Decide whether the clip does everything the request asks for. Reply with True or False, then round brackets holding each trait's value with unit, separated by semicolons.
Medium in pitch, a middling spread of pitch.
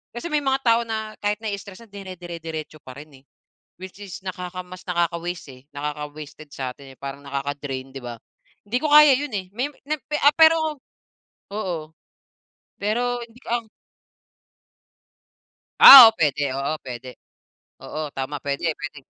False (180 Hz; 7.6 semitones)